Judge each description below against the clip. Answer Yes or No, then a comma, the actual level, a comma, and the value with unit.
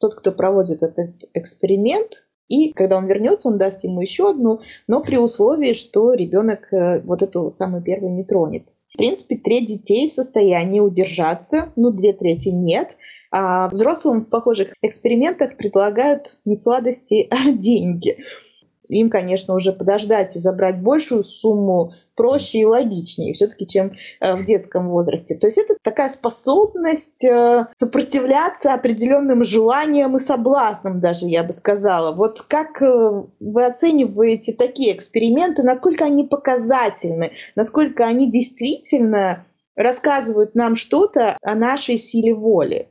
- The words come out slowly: No, average, 135 wpm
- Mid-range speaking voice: No, high, 225 Hz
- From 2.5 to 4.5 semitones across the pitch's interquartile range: No, wide, 5.5 semitones